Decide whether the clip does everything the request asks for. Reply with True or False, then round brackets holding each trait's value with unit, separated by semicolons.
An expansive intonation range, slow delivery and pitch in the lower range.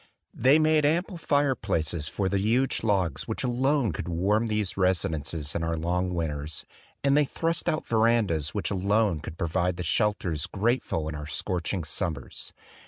False (6.2 semitones; 170 wpm; 95 Hz)